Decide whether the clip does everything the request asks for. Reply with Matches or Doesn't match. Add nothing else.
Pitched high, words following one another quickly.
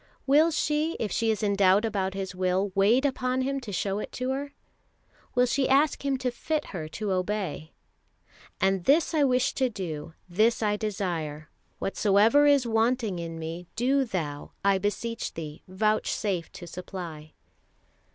Doesn't match